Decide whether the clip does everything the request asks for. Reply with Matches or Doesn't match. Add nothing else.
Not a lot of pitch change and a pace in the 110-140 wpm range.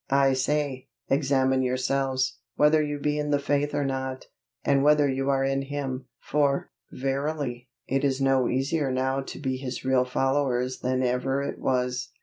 Doesn't match